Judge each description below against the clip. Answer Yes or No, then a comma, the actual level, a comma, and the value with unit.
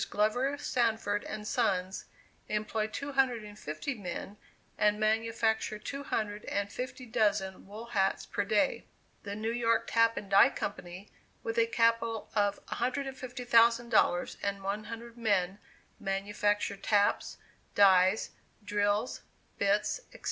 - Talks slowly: Yes, slow, 125 wpm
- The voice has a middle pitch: No, high, 215 Hz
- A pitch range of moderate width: No, narrow, 2.3 semitones